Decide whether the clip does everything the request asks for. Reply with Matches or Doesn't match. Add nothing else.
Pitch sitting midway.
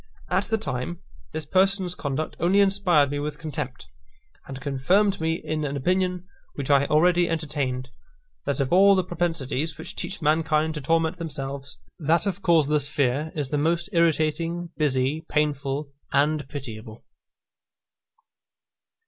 Matches